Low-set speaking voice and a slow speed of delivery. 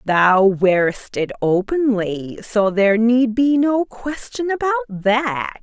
No: high, 230 Hz; slow, 130 wpm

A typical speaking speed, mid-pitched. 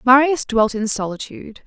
No: average, 145 wpm; high, 235 Hz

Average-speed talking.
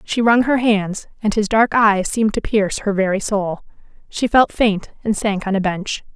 No: fast, 215 wpm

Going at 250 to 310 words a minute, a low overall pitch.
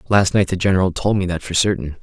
Yes: fast, 265 wpm; very low, 95 Hz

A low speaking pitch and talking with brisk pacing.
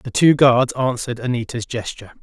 No: low, 125 Hz; average, 160 wpm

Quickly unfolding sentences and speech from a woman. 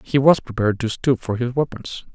No: fast, 225 wpm; male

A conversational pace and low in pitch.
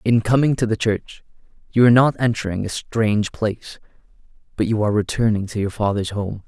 Yes: average, 185 wpm; low, 110 Hz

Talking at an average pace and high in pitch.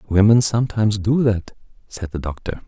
No: average, 155 wpm; low, 105 Hz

